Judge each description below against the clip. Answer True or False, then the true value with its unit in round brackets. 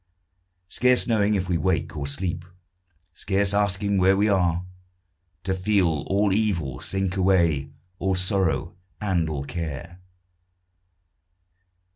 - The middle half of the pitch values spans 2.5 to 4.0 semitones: True (3.0 semitones)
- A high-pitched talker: False (95 Hz)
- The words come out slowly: True (115 wpm)